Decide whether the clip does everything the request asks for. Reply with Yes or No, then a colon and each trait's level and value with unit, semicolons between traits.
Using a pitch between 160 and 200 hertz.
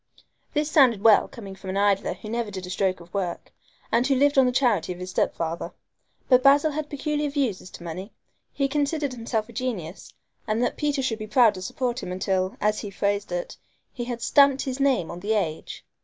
No: high, 230 Hz